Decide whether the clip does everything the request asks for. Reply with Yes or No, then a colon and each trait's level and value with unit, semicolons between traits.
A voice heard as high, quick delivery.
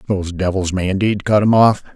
No: low, 100 Hz; fast, 215 wpm